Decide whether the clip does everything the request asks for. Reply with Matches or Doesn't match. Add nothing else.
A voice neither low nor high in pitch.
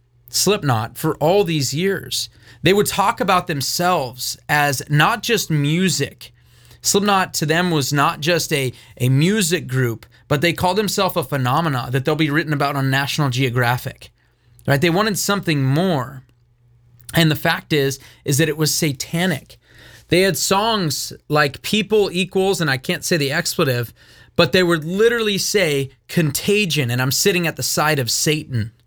Matches